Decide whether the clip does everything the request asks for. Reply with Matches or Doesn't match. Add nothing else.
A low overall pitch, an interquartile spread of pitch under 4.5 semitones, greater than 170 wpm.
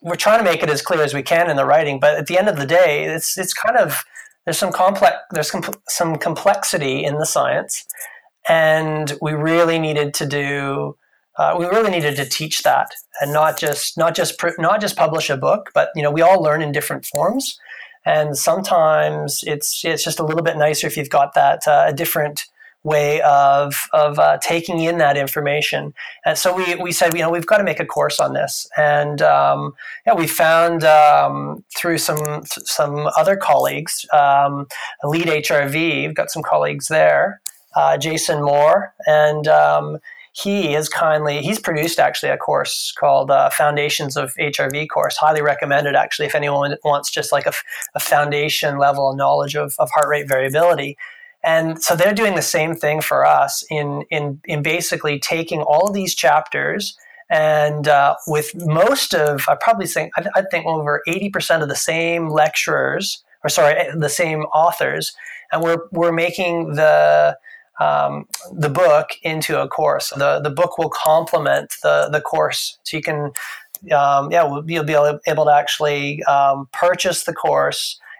Doesn't match